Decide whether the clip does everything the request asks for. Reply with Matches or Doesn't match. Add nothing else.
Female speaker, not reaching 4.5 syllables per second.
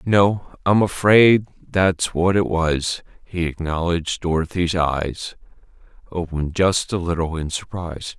Doesn't match